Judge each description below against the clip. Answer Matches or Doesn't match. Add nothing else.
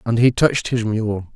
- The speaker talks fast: Matches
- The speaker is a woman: Doesn't match